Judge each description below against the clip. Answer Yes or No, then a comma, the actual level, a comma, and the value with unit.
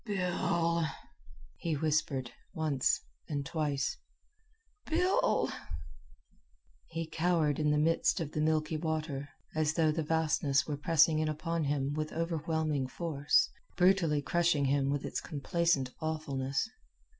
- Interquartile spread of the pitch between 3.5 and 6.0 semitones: No, narrow, 2.4 semitones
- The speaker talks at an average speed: No, slow, 120 wpm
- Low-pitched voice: No, medium, 155 Hz